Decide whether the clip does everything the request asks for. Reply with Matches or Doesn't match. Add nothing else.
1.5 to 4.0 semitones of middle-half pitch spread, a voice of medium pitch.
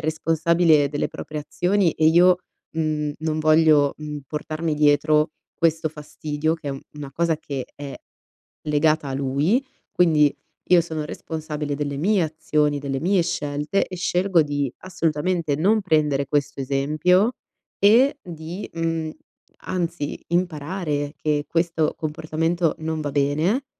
Matches